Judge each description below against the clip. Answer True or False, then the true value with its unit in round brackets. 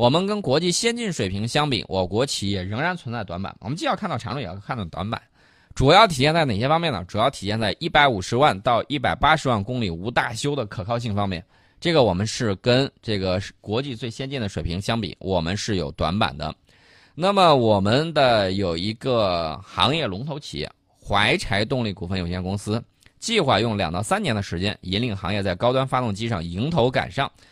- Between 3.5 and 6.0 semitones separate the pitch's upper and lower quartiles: True (5.5 semitones)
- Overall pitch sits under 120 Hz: True (110 Hz)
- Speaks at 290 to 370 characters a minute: True (320 characters per minute)